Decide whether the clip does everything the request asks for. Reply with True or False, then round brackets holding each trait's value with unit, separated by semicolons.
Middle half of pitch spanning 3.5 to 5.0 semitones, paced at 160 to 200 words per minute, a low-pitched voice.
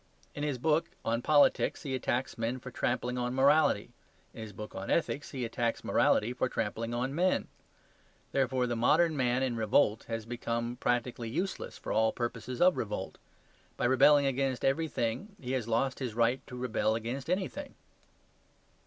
False (2.9 semitones; 165 wpm; 125 Hz)